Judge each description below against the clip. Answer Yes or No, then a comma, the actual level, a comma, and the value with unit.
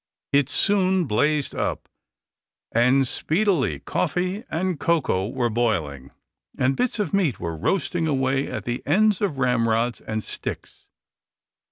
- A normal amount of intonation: No, wide, 7.6 semitones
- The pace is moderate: No, slow, 130 wpm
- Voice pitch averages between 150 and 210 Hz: No, low, 135 Hz